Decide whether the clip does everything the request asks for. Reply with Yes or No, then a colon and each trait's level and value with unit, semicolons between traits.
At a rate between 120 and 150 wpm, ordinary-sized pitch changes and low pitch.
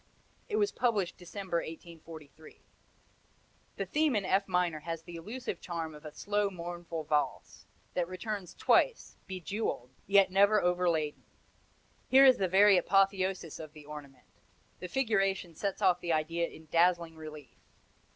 No: average, 140 wpm; average, 3.5 semitones; medium, 180 Hz